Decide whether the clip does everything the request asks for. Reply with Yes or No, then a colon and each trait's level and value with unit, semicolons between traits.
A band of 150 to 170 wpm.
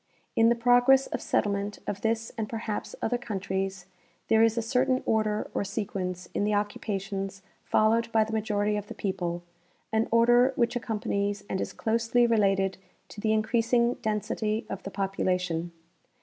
Yes: average, 165 wpm